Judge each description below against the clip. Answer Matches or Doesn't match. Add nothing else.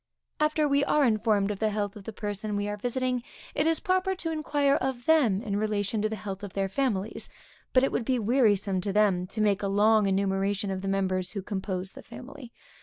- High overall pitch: Matches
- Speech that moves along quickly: Matches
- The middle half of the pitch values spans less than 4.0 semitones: Doesn't match